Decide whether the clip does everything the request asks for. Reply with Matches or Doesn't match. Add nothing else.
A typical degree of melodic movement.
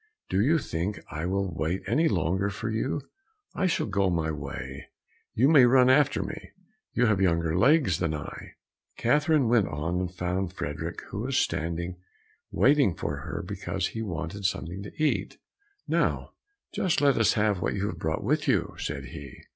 Doesn't match